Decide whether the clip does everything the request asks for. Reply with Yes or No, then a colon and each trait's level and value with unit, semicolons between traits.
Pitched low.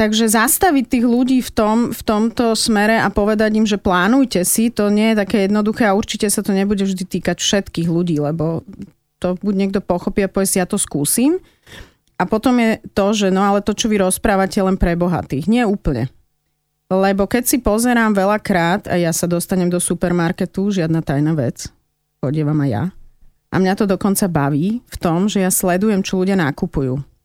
No: high, 195 Hz